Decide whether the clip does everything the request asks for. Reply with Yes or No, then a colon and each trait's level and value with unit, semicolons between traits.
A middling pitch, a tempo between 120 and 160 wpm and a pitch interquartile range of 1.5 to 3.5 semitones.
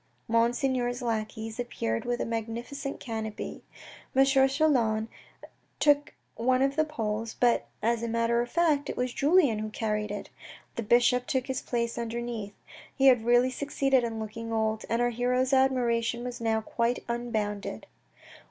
No: high, 240 Hz; average, 155 wpm; narrow, 2.5 semitones